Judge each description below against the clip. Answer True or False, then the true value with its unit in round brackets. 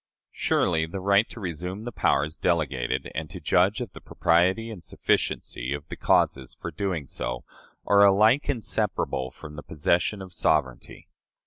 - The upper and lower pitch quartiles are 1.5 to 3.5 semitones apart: False (5.2 semitones)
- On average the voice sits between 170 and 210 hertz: False (90 Hz)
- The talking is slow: False (155 wpm)